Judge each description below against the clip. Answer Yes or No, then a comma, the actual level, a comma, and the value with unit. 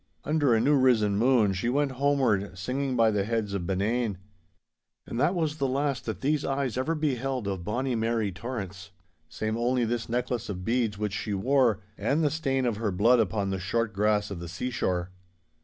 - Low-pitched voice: Yes, low, 115 Hz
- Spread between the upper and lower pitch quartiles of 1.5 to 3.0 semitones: No, average, 4.5 semitones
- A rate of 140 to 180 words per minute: No, average, 190 wpm